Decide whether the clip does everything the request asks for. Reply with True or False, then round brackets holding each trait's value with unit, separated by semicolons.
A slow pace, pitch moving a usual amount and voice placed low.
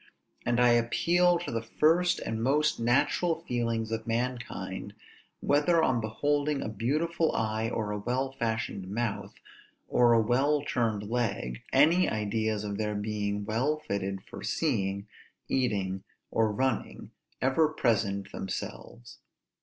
True (130 wpm; 4.6 semitones; 115 Hz)